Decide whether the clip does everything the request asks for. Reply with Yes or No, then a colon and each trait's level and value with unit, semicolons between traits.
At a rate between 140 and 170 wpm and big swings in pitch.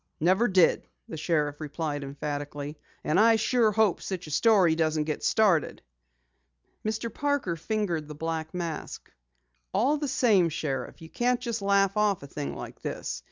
Yes: average, 160 wpm; wide, 6.1 semitones